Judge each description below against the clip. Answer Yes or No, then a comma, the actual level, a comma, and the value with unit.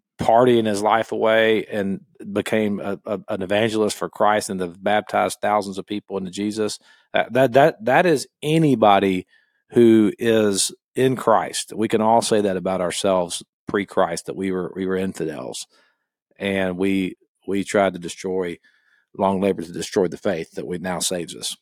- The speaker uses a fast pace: No, average, 170 wpm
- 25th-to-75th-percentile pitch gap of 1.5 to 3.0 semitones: Yes, average, 2.7 semitones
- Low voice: Yes, low, 100 Hz